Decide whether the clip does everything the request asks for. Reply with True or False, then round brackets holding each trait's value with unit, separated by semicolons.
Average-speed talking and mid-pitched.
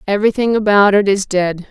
False (175 wpm; 200 Hz)